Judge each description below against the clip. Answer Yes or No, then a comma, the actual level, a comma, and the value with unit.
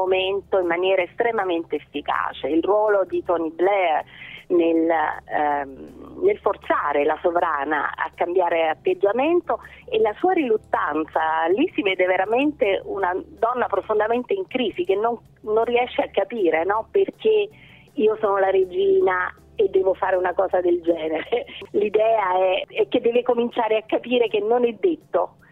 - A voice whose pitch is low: No, high, 210 Hz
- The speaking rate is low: No, average, 145 wpm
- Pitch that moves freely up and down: Yes, wide, 8.3 semitones